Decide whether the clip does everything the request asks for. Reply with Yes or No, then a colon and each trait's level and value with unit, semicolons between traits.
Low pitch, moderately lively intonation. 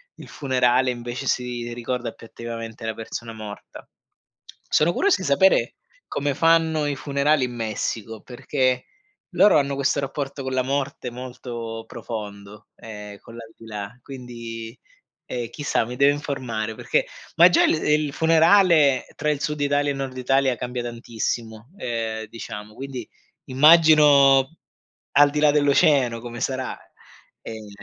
Yes: low, 130 Hz; average, 3.7 semitones